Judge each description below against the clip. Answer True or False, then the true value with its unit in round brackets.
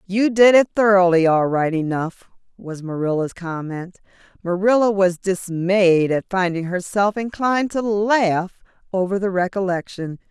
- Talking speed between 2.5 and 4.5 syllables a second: True (4.4 syllables/s)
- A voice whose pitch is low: False (190 Hz)